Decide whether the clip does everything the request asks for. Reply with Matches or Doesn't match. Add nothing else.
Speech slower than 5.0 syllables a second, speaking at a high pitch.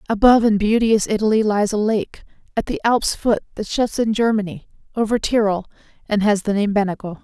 Doesn't match